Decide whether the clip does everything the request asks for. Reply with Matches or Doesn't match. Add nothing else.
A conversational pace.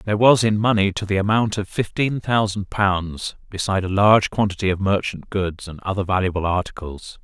Matches